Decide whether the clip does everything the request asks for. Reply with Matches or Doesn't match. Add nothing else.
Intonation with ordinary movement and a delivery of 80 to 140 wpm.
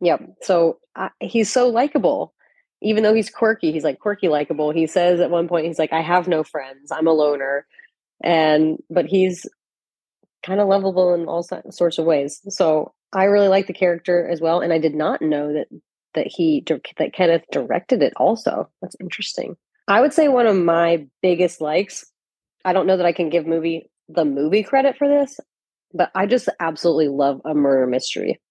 Doesn't match